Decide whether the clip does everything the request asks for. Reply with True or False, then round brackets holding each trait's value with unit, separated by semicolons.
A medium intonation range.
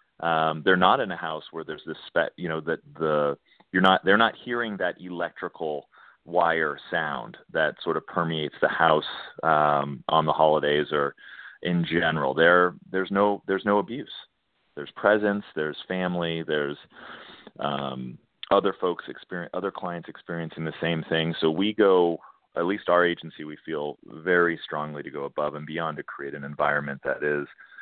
True (3.3 semitones)